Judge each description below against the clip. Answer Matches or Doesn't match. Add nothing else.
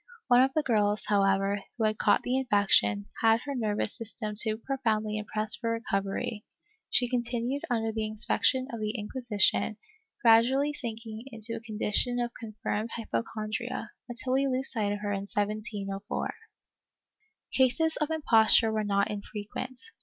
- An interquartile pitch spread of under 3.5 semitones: Matches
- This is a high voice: Matches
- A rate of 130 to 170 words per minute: Matches